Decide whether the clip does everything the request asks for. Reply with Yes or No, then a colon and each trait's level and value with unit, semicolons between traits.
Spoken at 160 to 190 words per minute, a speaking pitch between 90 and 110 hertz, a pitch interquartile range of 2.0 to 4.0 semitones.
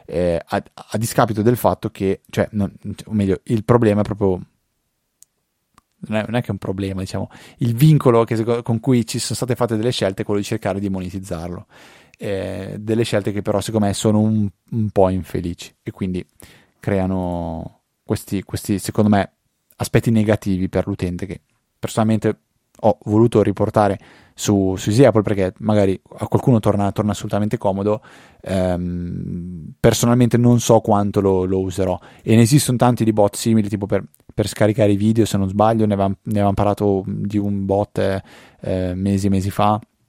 Yes: fast, 170 wpm; low, 105 Hz; average, 2.7 semitones